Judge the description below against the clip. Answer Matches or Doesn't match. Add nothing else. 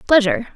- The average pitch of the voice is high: Matches